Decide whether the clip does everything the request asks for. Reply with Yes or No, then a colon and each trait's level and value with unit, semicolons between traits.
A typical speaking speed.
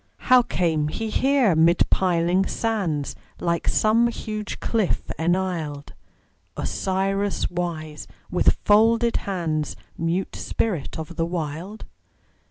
No: slow, 105 wpm